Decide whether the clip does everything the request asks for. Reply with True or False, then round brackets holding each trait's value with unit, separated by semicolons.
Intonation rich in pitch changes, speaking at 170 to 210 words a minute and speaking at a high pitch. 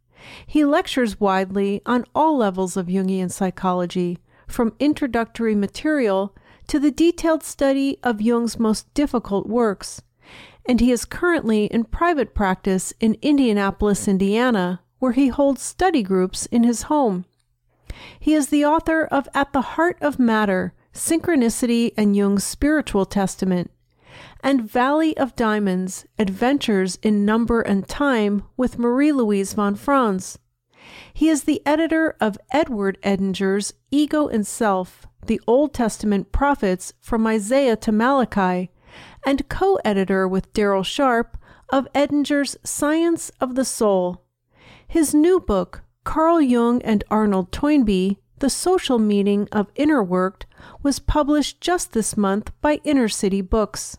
False (6.3 semitones; 135 wpm; 230 Hz)